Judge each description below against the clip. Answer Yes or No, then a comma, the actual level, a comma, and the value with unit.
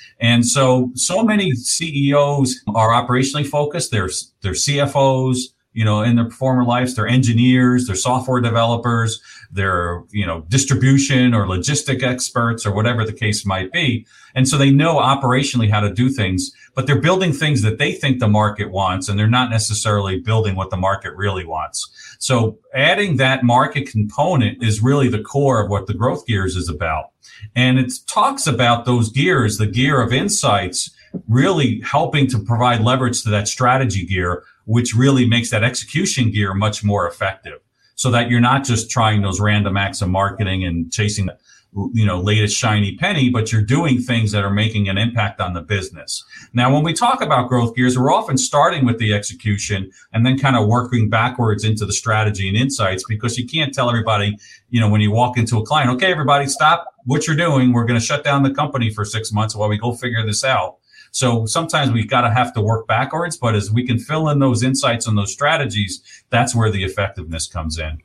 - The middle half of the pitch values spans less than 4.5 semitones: Yes, average, 3.8 semitones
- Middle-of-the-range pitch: No, low, 120 Hz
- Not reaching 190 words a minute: No, average, 195 wpm